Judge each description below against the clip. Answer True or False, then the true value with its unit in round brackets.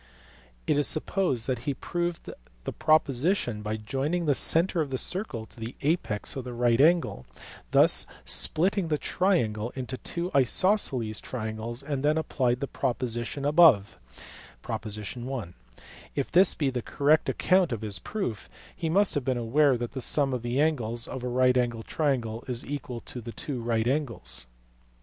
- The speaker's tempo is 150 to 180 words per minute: True (165 wpm)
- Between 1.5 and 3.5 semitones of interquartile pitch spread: False (4.8 semitones)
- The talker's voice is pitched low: True (130 Hz)